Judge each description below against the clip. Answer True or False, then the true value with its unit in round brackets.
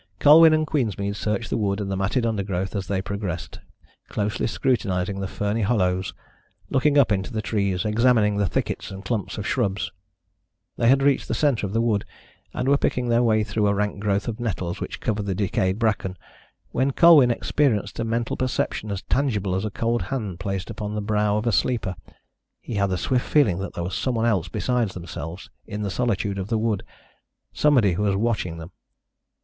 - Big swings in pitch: False (3.4 semitones)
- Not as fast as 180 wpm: False (195 wpm)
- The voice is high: False (105 Hz)